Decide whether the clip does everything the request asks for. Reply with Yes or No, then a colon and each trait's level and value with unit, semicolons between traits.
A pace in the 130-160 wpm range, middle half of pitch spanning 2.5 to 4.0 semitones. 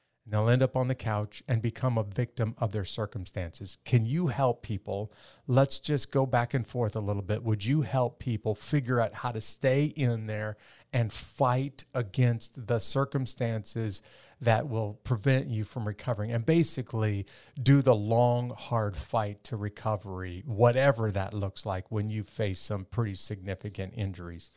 No: average, 170 wpm; average, 3.4 semitones